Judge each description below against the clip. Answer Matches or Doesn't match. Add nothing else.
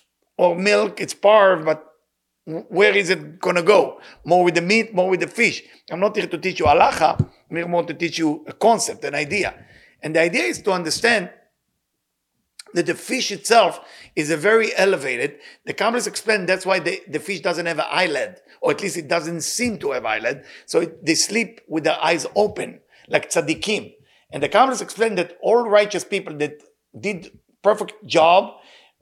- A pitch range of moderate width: Matches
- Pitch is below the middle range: Doesn't match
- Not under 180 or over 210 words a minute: Matches